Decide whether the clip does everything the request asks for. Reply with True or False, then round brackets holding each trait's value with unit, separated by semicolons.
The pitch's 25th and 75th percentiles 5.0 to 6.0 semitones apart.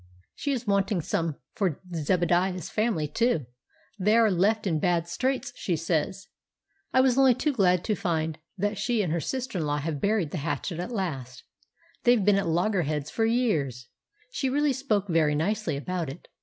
True (5.6 semitones)